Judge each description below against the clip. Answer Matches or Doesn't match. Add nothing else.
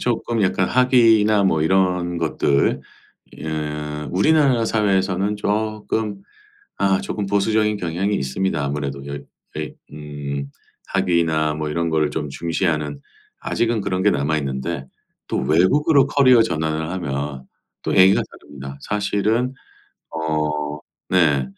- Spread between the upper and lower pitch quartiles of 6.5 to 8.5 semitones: Doesn't match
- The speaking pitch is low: Matches